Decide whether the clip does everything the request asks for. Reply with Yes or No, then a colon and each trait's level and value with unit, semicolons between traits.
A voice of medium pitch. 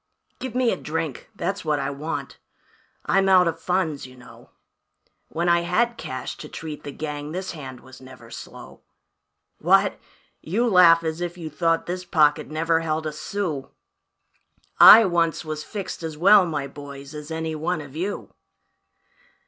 Yes: medium, 160 Hz